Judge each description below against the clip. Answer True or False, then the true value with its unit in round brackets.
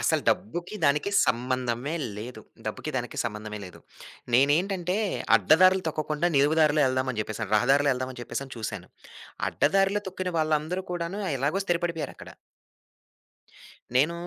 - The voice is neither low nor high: True (145 Hz)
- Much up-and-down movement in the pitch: True (5.7 semitones)